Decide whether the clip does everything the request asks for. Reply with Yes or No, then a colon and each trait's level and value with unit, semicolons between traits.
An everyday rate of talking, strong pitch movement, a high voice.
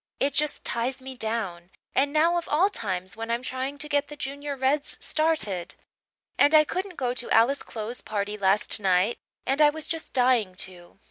Yes: average, 190 wpm; wide, 5.7 semitones; very high, 260 Hz